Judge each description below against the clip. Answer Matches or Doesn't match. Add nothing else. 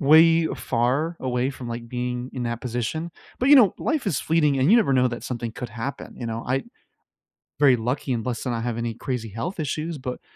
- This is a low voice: Matches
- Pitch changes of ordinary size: Matches